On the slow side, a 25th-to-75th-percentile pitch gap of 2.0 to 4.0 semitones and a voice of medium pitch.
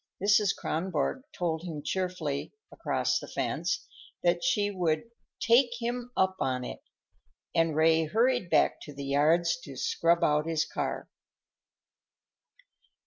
No: slow, 130 wpm; average, 4.8 semitones; medium, 170 Hz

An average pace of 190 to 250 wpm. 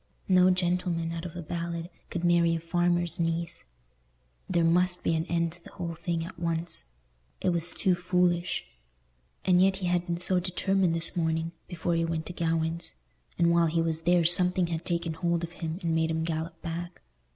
Yes: average, 195 wpm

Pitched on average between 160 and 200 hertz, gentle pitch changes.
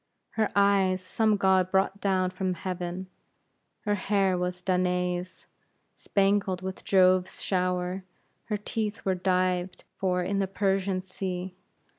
Yes: medium, 185 Hz; narrow, 1.3 semitones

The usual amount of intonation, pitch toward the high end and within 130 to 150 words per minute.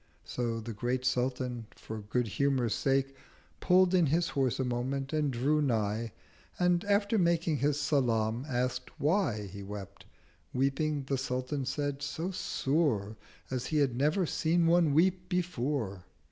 No: average, 4.6 semitones; low, 135 Hz; average, 145 wpm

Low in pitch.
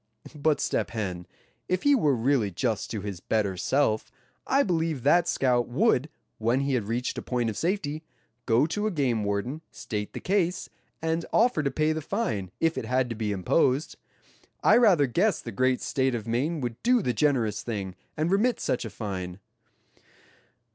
Yes: low, 130 Hz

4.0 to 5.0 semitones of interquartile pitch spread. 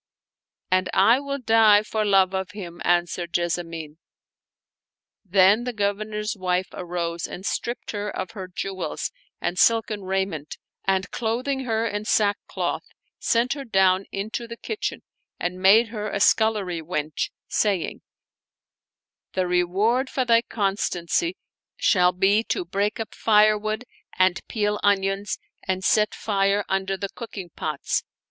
No: average, 3.0 semitones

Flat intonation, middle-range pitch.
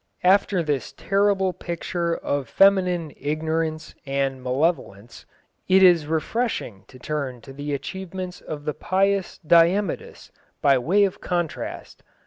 No: average, 4.7 semitones; medium, 165 Hz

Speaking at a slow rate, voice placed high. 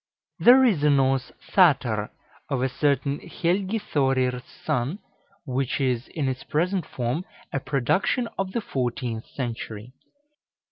No: slow, 130 wpm; low, 135 Hz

